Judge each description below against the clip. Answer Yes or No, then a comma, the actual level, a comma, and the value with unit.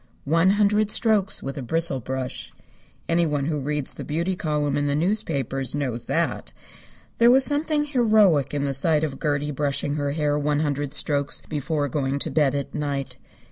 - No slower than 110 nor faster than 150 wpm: No, average, 175 wpm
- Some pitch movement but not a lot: Yes, average, 3.2 semitones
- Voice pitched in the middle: Yes, medium, 150 Hz